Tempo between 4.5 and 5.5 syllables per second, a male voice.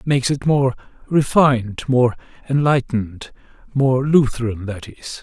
Yes: 4.7 syllables/s; male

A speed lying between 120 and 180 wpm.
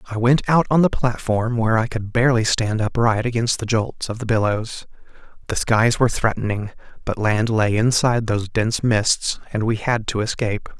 No: average, 190 wpm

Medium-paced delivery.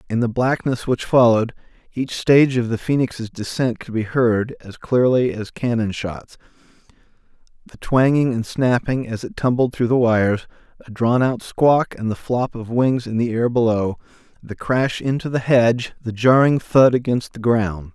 Yes: average, 175 wpm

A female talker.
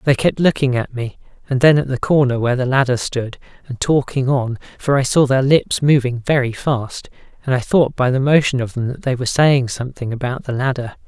No: male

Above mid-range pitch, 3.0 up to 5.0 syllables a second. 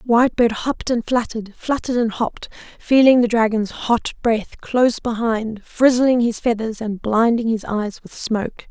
Yes: high, 230 Hz; 4.8 syllables/s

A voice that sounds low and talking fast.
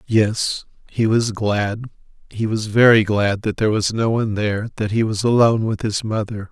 No: low, 110 Hz; average, 195 wpm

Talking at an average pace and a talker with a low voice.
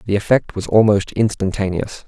Yes: average, 145 wpm; low, 105 Hz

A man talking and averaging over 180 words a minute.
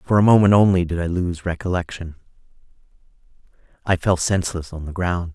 No: male; average, 155 wpm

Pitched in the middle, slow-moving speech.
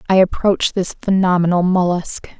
Yes: medium, 180 Hz; slow, 125 wpm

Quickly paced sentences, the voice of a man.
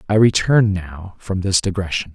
No: average, 170 wpm; male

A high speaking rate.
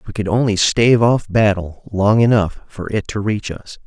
Yes: fast, 215 wpm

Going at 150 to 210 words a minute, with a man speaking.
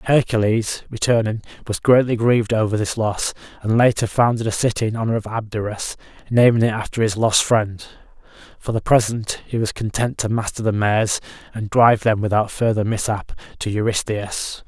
Yes: average, 170 wpm; male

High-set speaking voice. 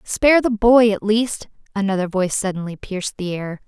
Yes: high, 205 Hz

